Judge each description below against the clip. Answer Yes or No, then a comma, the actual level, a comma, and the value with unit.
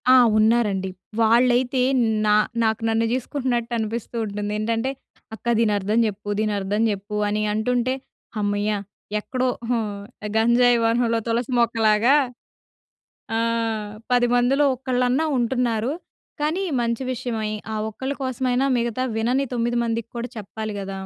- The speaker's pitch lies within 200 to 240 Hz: Yes, high, 230 Hz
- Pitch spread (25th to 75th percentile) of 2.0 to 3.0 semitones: Yes, narrow, 2.5 semitones